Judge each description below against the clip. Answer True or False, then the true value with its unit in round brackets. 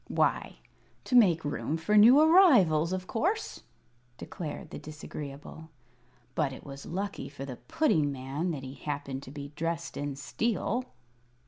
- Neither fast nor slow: True (145 wpm)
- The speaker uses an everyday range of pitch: False (6.3 semitones)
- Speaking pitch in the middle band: True (160 Hz)